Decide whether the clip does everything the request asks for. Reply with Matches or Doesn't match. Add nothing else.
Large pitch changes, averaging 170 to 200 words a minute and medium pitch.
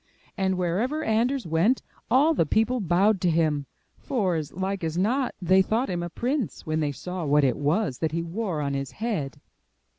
Matches